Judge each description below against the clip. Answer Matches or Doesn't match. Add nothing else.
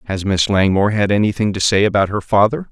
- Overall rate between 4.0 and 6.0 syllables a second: Doesn't match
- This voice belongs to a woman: Doesn't match